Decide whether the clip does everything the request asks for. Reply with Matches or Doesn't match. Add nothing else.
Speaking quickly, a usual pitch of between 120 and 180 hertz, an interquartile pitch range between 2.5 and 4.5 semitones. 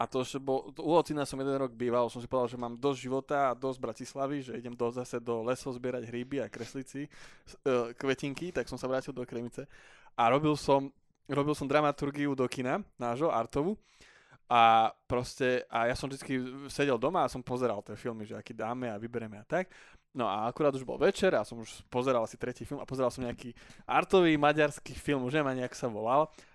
Matches